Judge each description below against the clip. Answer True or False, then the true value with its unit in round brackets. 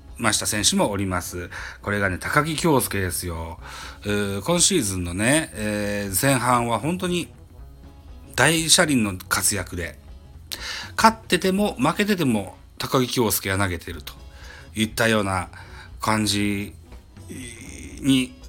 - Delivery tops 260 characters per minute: False (245 characters per minute)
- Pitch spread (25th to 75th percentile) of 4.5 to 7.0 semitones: True (6.1 semitones)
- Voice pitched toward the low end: True (100 Hz)